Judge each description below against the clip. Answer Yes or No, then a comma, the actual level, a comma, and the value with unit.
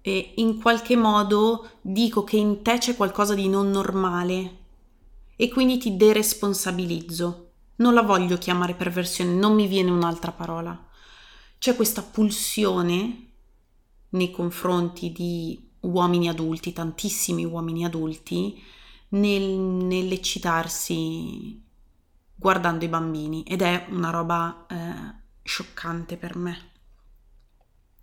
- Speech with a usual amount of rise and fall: Yes, average, 3.5 semitones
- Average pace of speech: No, slow, 110 wpm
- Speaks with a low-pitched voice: No, medium, 180 Hz